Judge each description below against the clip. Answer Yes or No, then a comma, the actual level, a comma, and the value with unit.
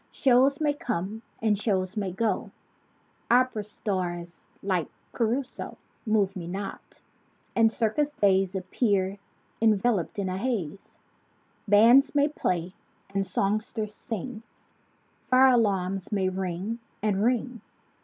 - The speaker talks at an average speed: No, slow, 120 wpm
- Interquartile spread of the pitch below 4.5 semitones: Yes, average, 3.9 semitones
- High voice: Yes, high, 210 Hz